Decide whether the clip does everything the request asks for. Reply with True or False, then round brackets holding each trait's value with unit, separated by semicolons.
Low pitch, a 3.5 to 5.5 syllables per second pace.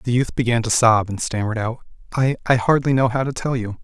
False (120 Hz; 6.1 syllables/s)